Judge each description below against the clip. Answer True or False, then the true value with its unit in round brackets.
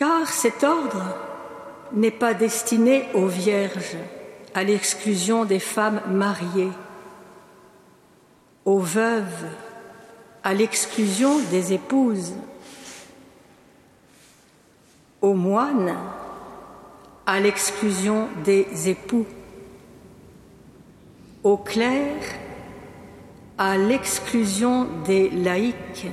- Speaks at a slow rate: True (70 wpm)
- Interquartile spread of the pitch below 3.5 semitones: True (3.0 semitones)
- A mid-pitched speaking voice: False (205 Hz)